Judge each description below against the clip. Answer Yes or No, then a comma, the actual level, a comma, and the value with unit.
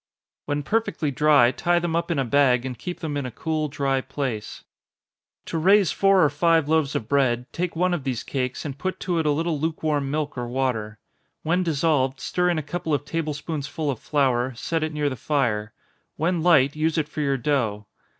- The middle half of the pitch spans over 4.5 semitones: No, average, 3.6 semitones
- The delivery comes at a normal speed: No, fast, 210 wpm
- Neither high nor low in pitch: Yes, medium, 145 Hz